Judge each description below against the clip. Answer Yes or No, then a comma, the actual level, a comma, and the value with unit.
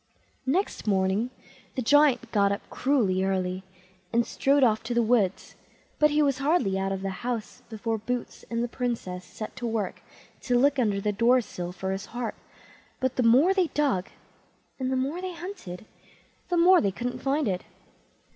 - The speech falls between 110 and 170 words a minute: No, average, 180 wpm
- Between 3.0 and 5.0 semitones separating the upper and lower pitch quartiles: No, wide, 5.6 semitones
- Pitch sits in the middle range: No, high, 235 Hz